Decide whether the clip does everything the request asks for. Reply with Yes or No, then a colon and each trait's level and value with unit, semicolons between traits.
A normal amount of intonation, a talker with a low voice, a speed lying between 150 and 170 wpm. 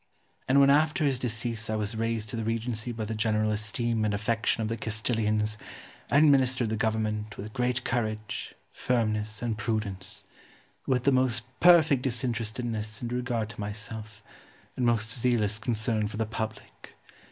No: narrow, 2.3 semitones; low, 110 Hz; average, 160 wpm